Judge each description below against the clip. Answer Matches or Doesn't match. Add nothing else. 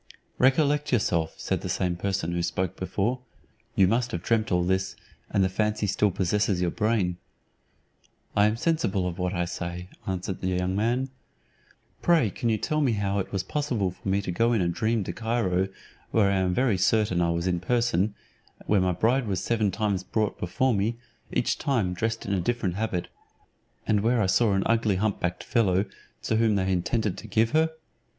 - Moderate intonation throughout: Matches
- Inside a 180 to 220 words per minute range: Matches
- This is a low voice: Matches